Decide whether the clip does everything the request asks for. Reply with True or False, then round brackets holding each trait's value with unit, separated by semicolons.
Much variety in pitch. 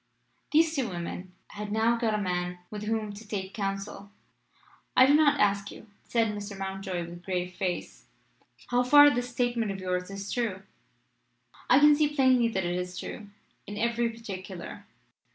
False (4.1 semitones)